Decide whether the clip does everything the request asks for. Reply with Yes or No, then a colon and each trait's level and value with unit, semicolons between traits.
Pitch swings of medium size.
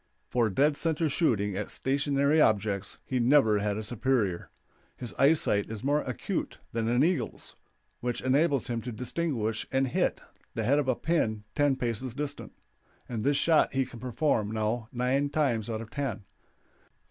Yes: average, 4.4 semitones